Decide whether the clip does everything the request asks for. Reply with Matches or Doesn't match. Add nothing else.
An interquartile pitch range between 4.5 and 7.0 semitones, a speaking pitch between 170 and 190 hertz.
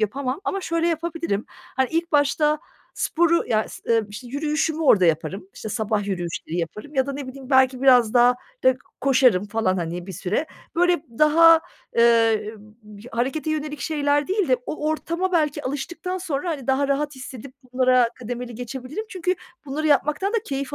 Doesn't match